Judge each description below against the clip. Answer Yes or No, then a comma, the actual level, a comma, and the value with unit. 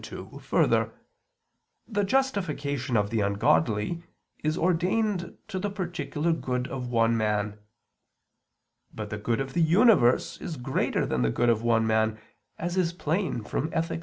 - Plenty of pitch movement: Yes, wide, 7.5 semitones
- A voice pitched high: No, low, 135 Hz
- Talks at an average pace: Yes, average, 150 wpm